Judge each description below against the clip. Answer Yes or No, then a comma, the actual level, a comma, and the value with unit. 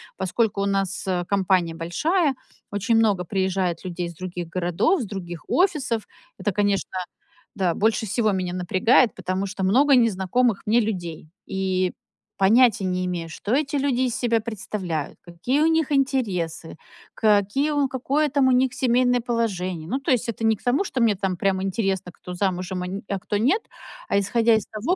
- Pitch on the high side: Yes, high, 205 Hz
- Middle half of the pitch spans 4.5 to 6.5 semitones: Yes, average, 5.1 semitones